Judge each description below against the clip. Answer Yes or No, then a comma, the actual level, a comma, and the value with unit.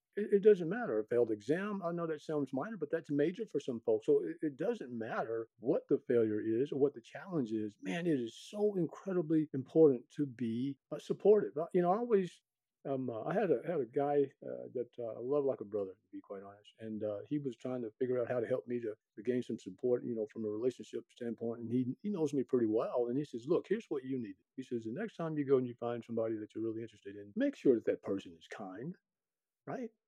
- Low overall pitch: Yes, low, 130 Hz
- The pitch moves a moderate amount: No, wide, 6.6 semitones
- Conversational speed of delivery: No, fast, 250 wpm